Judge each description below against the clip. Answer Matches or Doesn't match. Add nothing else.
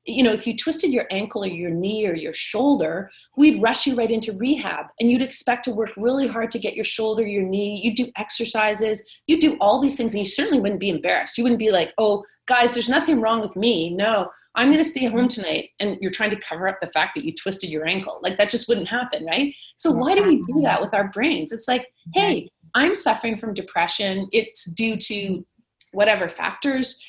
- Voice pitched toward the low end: Doesn't match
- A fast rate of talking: Matches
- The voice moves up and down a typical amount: Matches